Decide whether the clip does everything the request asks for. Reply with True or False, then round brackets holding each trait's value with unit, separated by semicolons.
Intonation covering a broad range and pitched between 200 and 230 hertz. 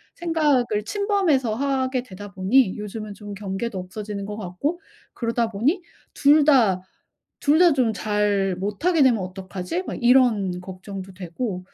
True (5.7 semitones; 215 Hz)